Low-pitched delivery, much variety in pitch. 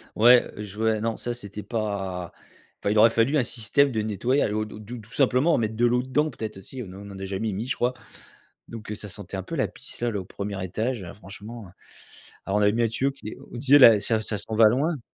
No: low, 110 Hz; average, 3.0 semitones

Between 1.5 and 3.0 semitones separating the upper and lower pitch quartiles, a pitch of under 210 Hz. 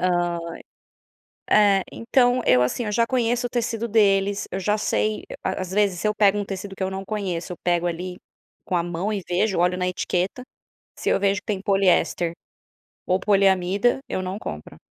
Yes: average, 2.7 semitones; high, 195 Hz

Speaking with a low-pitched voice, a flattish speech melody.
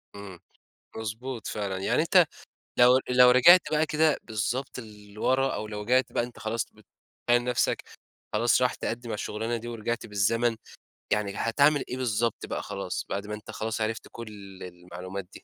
No: low, 115 Hz; average, 3.0 semitones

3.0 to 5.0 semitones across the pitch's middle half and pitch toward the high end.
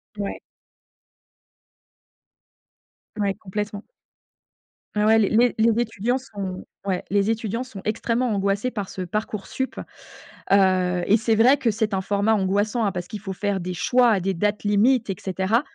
No: narrow, 2.6 semitones; high, 205 Hz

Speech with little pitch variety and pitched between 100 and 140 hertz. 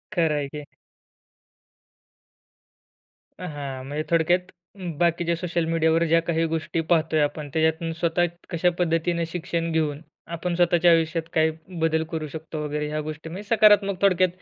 No: narrow, 1.6 semitones; medium, 165 Hz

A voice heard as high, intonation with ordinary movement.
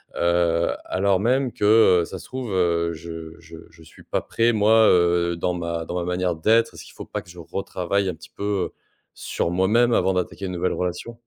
No: very low, 90 Hz; average, 3.4 semitones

